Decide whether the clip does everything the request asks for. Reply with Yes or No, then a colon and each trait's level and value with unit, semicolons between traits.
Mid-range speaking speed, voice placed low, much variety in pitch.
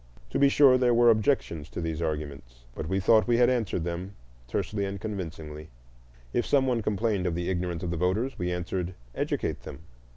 Yes: average, 190 wpm; very low, 95 Hz; wide, 5.7 semitones